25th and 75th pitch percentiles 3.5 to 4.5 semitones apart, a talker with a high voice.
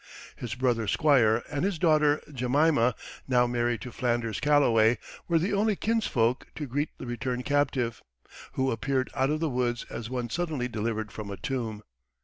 No: average, 3.9 semitones; low, 125 Hz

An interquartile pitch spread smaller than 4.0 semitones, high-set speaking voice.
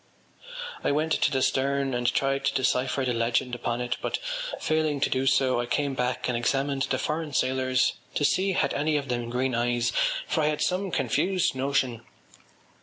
No: average, 2.9 semitones; low, 135 Hz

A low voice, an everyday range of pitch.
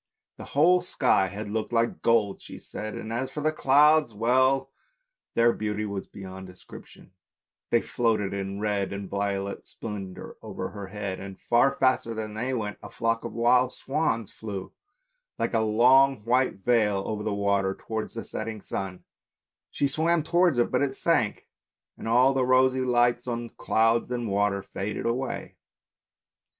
Yes: low, 115 Hz; average, 4.0 semitones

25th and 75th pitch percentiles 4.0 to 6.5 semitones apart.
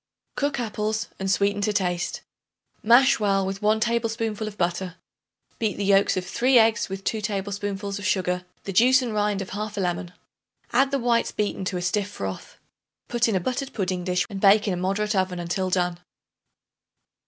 No: average, 2.8 semitones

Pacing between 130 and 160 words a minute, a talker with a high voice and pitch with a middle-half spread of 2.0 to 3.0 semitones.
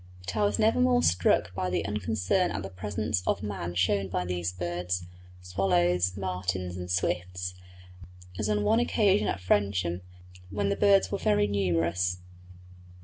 No: average, 155 wpm; very low, 95 Hz; narrow, 2.4 semitones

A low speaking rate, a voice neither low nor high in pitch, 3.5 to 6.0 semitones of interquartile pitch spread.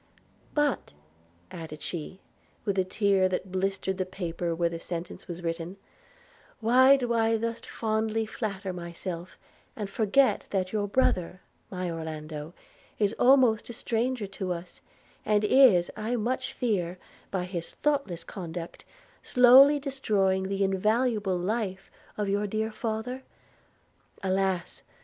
No: slow, 130 wpm; high, 195 Hz; average, 3.9 semitones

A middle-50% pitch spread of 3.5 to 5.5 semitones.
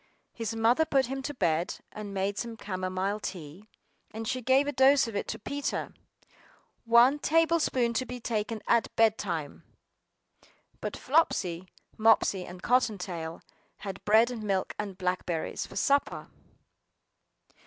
Yes: average, 4.9 semitones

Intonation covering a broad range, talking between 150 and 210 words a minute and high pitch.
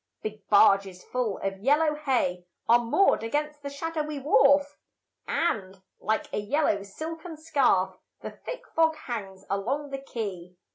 No: wide, 7.1 semitones; average, 140 wpm; very high, 255 Hz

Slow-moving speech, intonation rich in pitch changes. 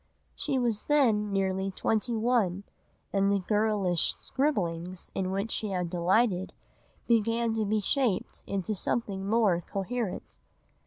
No: slow, 125 wpm; average, 3.3 semitones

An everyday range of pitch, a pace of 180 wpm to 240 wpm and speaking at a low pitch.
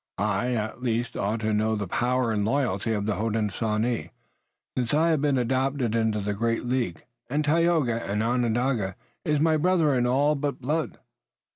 No: average, 4.3 semitones; average, 170 wpm; low, 120 Hz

